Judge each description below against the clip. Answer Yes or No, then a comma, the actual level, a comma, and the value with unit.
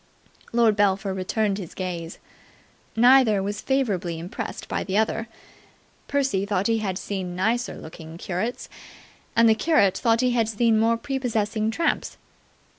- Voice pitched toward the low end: No, high, 215 Hz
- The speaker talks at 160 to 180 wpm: No, average, 140 wpm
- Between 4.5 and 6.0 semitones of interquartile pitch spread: No, average, 3.5 semitones